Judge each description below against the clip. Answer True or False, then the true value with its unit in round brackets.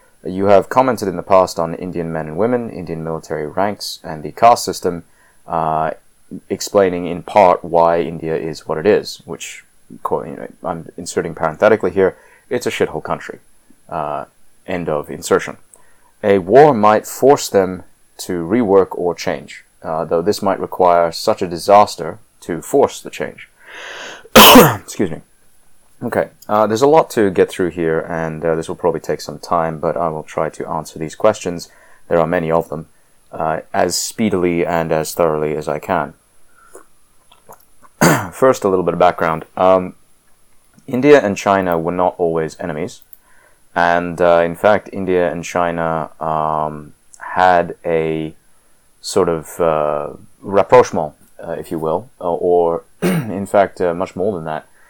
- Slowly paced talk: False (160 wpm)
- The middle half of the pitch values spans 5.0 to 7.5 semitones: False (3.1 semitones)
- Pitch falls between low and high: False (85 Hz)